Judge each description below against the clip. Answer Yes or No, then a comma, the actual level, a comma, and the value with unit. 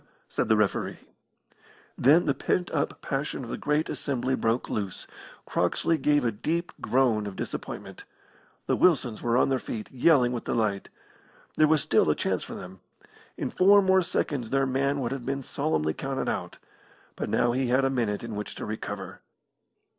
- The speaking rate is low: No, average, 175 wpm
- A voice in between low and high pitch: No, low, 130 Hz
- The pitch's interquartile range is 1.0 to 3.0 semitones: No, average, 4.5 semitones